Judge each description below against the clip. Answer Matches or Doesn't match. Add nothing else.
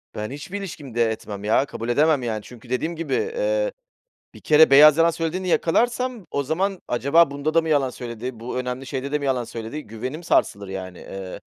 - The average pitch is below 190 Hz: Matches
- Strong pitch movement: Matches